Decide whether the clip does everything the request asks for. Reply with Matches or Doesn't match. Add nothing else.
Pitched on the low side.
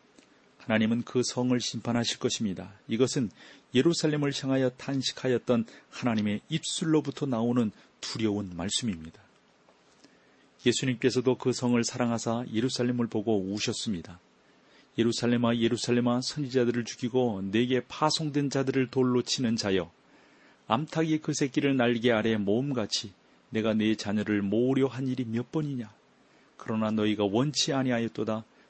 Matches